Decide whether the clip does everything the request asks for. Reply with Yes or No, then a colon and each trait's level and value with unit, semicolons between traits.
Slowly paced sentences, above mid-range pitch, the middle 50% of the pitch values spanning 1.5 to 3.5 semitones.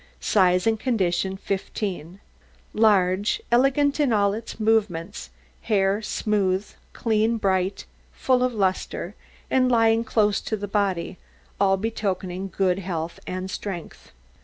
Yes: slow, 120 wpm; high, 200 Hz; average, 3.2 semitones